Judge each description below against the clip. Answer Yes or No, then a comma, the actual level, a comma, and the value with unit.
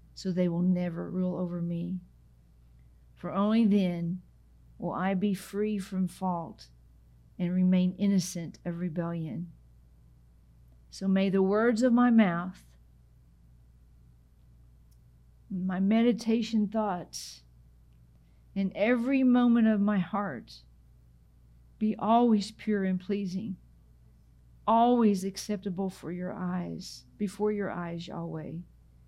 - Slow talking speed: Yes, slow, 105 wpm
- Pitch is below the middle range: No, medium, 175 Hz